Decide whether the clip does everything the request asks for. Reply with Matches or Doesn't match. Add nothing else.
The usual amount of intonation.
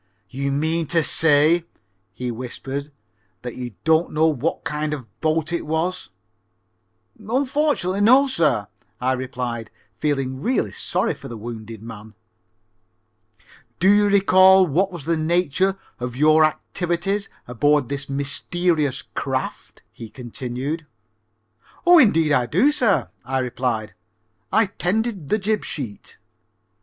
Doesn't match